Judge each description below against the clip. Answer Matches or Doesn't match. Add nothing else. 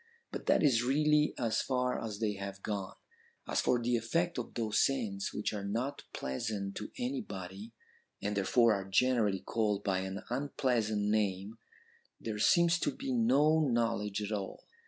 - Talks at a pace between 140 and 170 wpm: Matches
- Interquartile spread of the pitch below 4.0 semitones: Doesn't match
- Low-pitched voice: Matches